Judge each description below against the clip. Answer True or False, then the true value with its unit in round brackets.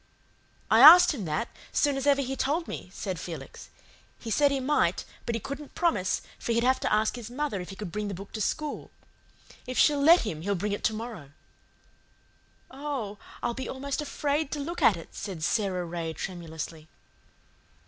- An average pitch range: False (6.8 semitones)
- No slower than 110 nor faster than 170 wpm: False (190 wpm)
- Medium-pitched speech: False (230 Hz)